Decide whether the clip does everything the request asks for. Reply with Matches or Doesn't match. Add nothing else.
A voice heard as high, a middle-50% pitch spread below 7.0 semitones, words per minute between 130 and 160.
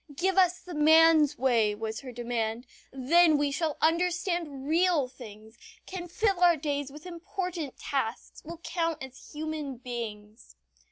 Matches